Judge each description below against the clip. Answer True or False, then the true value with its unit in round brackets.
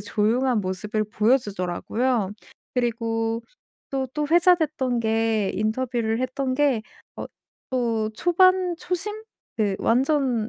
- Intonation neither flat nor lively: True (3.9 semitones)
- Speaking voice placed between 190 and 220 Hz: False (240 Hz)